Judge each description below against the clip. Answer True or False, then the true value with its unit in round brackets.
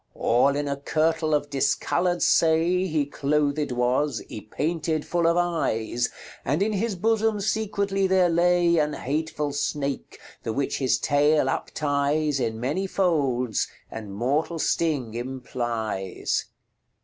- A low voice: False (150 Hz)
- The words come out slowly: True (125 wpm)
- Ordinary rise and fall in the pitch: True (4.5 semitones)